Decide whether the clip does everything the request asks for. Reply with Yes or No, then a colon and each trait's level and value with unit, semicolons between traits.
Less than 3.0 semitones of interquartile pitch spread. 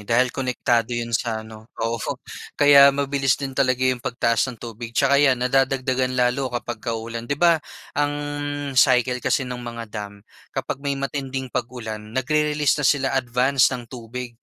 Yes: narrow, 2.6 semitones